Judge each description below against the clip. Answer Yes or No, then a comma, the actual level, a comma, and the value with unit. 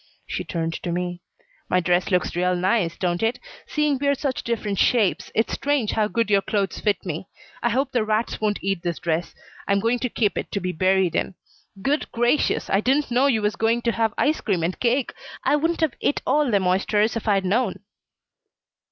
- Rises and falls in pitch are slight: No, average, 4.9 semitones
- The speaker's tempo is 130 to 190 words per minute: No, fast, 205 wpm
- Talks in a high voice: Yes, high, 210 Hz